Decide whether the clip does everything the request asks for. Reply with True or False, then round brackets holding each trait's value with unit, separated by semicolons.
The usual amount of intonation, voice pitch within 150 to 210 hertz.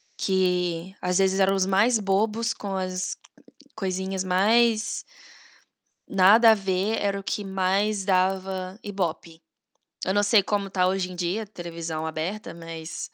False (2.0 semitones; 190 Hz)